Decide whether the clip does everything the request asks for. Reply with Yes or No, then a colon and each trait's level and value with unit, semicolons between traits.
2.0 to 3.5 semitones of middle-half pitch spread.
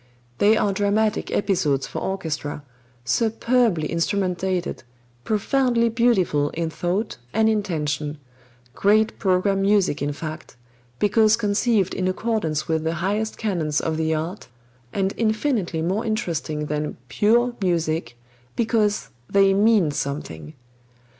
No: wide, 5.4 semitones